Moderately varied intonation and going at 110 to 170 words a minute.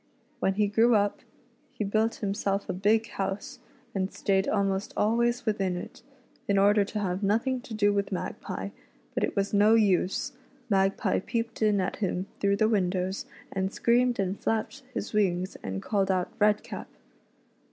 No: narrow, 2.2 semitones; average, 165 wpm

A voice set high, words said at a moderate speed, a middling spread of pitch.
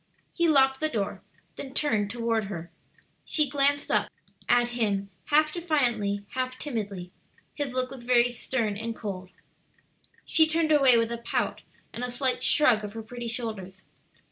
Yes: high, 240 Hz; average, 160 wpm; average, 4.4 semitones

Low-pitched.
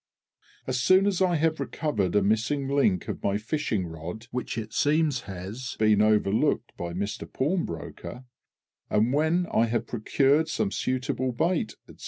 Yes: low, 120 Hz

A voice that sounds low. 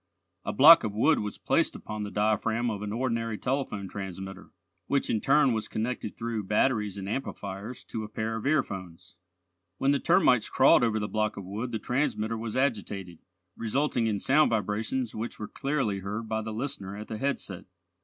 Yes: low, 110 Hz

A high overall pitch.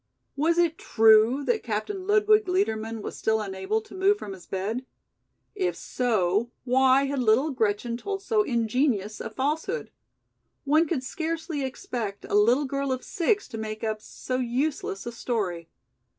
Yes: very high, 255 Hz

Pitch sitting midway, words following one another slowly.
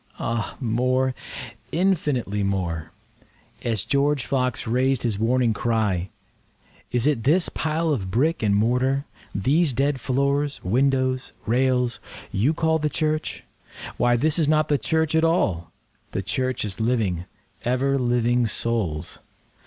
No: low, 125 Hz; slow, 115 wpm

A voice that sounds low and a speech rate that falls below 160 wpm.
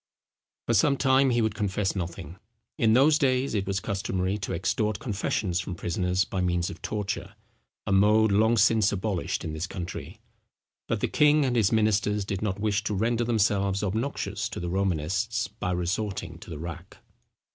No: low, 100 Hz; average, 175 wpm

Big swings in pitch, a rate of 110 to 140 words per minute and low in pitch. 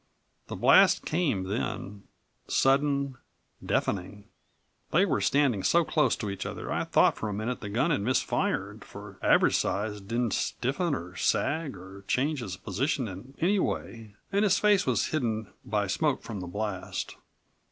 No: wide, 6.0 semitones; average, 160 wpm; low, 115 Hz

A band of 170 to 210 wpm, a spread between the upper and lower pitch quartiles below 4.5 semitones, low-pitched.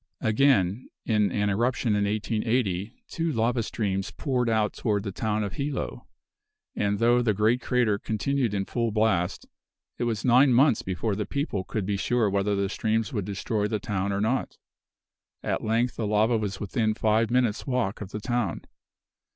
Yes: average, 175 wpm; average, 2.9 semitones; low, 110 Hz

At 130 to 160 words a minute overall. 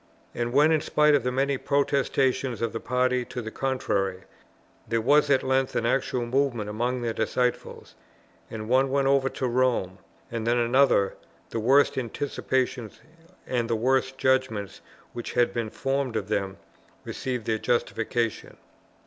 Yes: average, 155 wpm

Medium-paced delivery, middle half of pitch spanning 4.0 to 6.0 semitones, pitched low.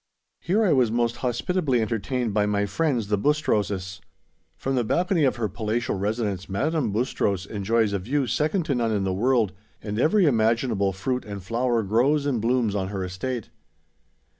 Yes: average, 170 wpm; average, 4.3 semitones; low, 115 Hz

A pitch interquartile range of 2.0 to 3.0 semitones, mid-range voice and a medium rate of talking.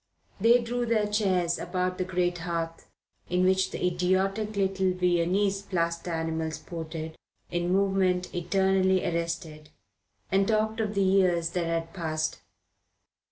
No: narrow, 2.5 semitones; medium, 180 Hz; slow, 130 wpm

